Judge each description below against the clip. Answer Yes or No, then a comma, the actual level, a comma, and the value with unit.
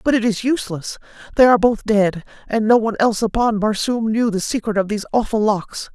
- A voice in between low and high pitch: No, high, 220 Hz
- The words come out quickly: Yes, fast, 210 wpm